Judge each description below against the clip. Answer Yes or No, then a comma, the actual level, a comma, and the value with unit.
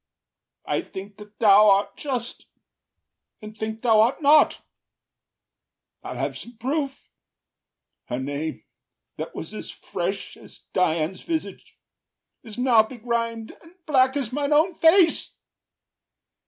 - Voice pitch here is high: Yes, high, 230 Hz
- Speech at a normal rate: No, slow, 120 wpm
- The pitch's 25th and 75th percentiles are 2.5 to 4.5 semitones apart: No, average, 5.1 semitones